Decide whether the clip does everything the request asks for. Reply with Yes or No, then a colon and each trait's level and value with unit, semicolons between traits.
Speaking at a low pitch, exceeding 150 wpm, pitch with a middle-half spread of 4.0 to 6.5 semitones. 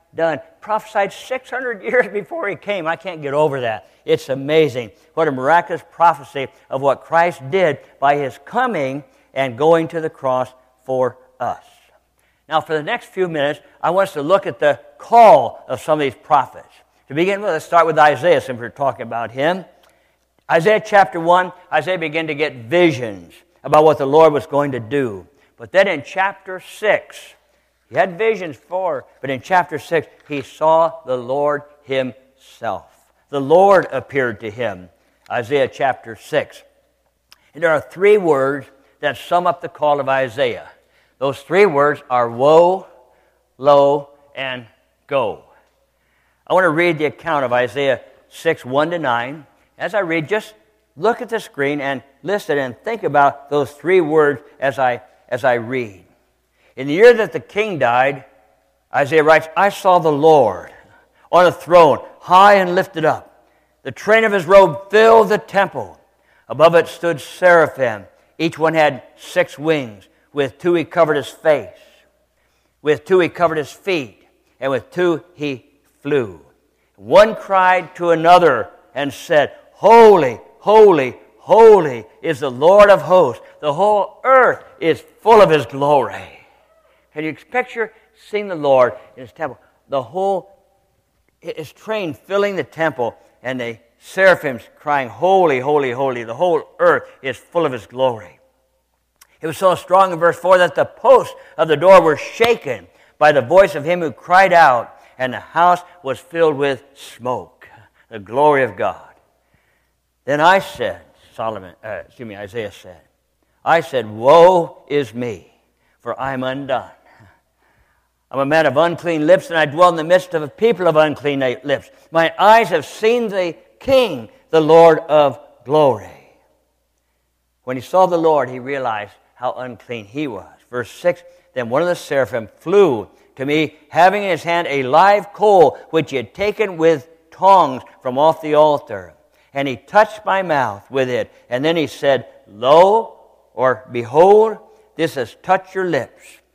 No: medium, 160 Hz; average, 165 wpm; wide, 5.4 semitones